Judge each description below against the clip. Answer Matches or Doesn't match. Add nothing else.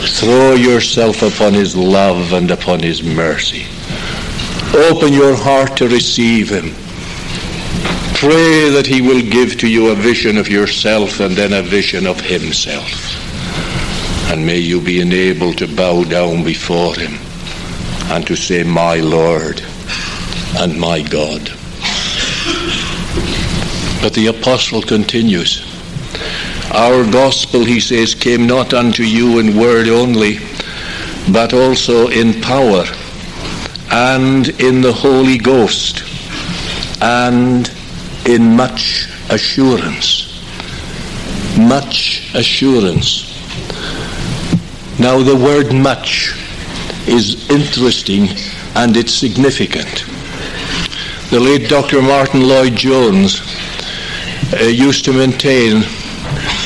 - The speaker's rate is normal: Doesn't match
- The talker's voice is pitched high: Doesn't match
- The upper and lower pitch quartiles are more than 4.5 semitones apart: Matches